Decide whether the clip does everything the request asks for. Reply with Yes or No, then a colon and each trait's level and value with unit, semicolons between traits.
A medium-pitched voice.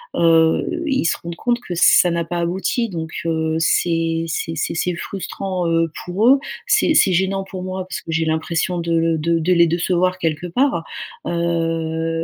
Yes: medium, 170 Hz